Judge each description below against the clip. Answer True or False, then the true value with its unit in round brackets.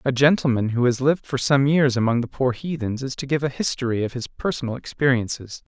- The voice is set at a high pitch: False (130 Hz)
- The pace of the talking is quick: True (220 wpm)